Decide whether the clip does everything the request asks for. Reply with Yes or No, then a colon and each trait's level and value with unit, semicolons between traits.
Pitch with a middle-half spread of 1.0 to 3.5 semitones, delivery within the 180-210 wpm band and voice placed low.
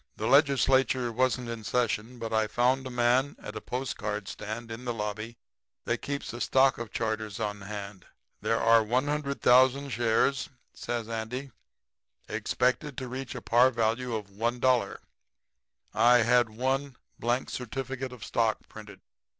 No: average, 2.8 semitones; average, 145 wpm; low, 120 Hz